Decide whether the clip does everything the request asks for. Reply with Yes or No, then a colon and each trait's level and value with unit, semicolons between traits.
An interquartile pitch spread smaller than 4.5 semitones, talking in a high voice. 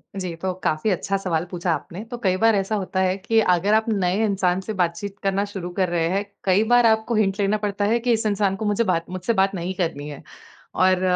Yes: narrow, 2.5 semitones; high, 195 Hz